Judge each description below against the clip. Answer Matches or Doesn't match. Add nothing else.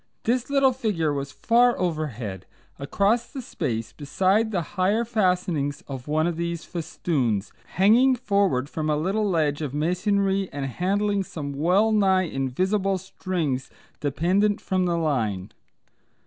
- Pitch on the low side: Doesn't match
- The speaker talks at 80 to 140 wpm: Matches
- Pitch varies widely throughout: Matches